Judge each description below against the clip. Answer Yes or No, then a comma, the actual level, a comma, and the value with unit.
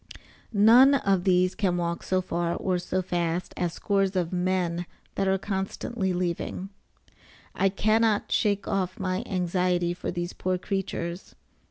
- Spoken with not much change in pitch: Yes, narrow, 1.8 semitones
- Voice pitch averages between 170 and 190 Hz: Yes, medium, 185 Hz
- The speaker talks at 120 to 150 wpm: Yes, average, 145 wpm